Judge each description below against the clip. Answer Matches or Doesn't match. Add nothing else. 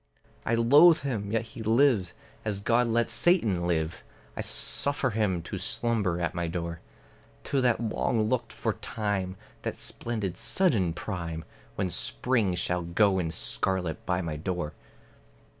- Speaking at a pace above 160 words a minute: Doesn't match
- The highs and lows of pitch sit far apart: Doesn't match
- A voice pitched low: Matches